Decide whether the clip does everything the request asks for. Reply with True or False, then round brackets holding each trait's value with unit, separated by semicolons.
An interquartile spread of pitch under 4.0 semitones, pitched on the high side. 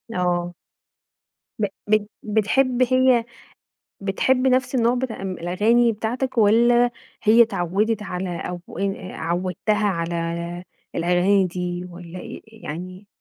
False (4.8 semitones; 205 Hz)